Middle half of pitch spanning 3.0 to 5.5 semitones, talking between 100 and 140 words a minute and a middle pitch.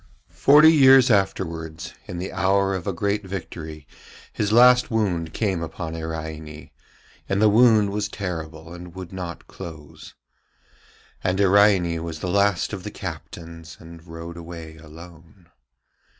No: average, 3.6 semitones; slow, 135 wpm; very low, 90 Hz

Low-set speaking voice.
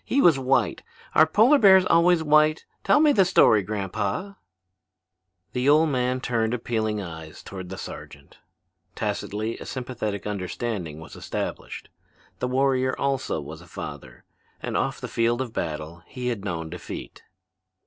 Yes: low, 120 Hz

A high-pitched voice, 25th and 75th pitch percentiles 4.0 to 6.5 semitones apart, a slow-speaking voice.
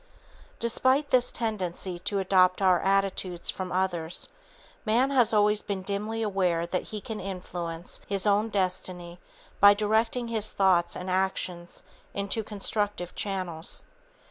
No: high, 195 Hz; average, 2.8 semitones; slow, 130 wpm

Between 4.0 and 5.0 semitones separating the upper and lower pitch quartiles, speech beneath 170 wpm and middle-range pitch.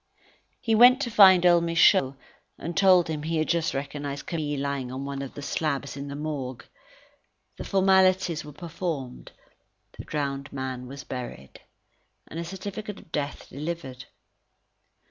Yes: average, 4.3 semitones; average, 150 wpm; medium, 150 Hz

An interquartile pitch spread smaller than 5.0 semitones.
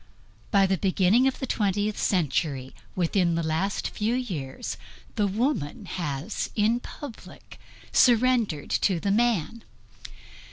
No: wide, 5.5 semitones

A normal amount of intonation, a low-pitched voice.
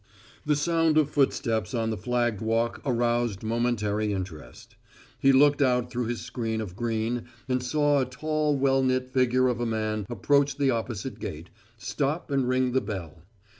Yes: average, 3.4 semitones; low, 125 Hz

